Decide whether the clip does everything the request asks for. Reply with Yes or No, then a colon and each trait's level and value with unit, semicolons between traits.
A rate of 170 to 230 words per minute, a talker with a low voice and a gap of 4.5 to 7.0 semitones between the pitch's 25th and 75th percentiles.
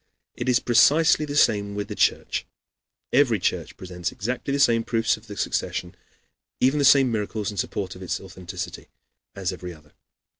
Yes: average, 180 wpm; low, 105 Hz; wide, 5.4 semitones